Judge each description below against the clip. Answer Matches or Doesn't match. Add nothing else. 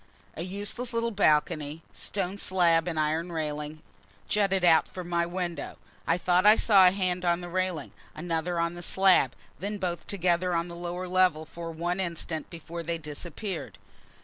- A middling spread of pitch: Doesn't match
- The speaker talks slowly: Doesn't match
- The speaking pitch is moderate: Matches